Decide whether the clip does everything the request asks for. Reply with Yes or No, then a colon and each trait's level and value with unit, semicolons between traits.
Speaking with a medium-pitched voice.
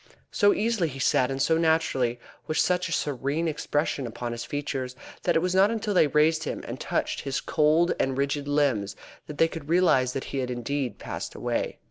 Yes: medium, 145 Hz